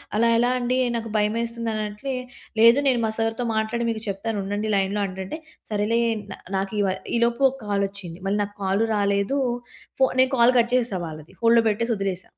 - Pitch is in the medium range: No, high, 220 Hz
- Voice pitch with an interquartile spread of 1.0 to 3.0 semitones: Yes, average, 2.7 semitones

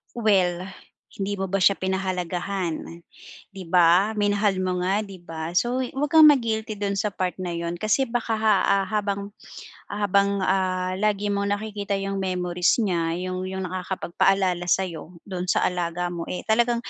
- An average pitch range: No, narrow, 2.2 semitones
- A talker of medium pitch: No, high, 195 Hz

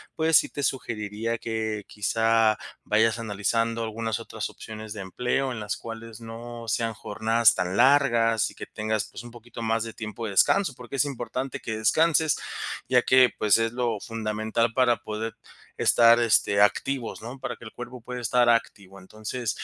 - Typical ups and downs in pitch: No, narrow, 1.9 semitones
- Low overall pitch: Yes, low, 115 Hz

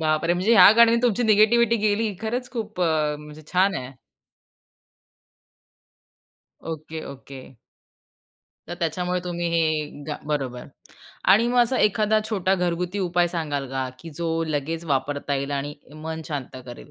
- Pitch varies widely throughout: Yes, wide, 5.8 semitones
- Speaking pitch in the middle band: Yes, medium, 170 Hz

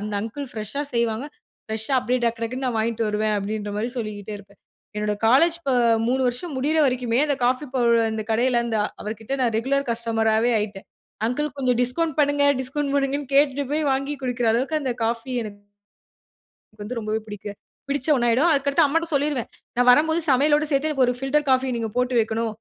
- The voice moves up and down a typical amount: Yes, average, 3.9 semitones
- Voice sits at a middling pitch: No, high, 245 Hz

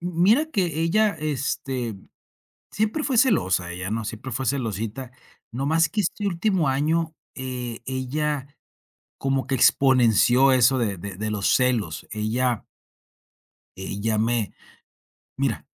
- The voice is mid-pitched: No, low, 130 Hz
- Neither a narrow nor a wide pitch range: No, wide, 6.1 semitones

